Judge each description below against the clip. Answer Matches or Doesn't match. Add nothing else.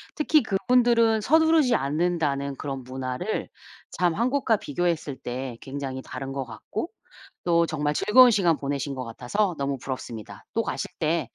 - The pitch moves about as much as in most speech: Doesn't match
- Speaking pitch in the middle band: Matches